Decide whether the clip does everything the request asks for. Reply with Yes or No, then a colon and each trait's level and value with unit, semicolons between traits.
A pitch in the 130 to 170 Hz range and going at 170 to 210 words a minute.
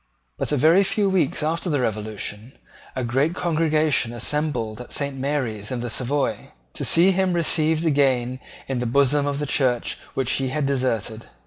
Yes: medium, 140 Hz; average, 175 wpm